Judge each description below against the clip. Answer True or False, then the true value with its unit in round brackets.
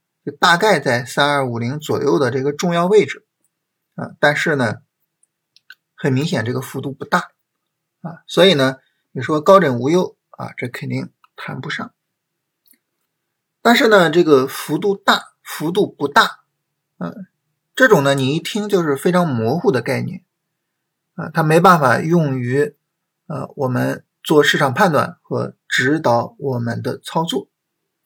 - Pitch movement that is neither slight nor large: True (4.5 semitones)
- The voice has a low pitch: False (160 Hz)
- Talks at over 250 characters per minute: False (210 characters per minute)